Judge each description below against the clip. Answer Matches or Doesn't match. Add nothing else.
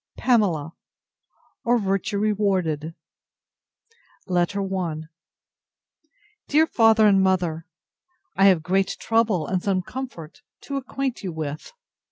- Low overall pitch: Doesn't match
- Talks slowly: Matches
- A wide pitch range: Doesn't match